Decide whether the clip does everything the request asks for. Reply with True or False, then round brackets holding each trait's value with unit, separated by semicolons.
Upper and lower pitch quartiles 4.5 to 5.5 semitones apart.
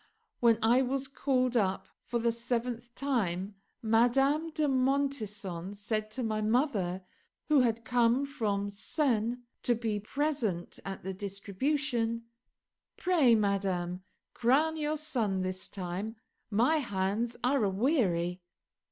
True (5.0 semitones)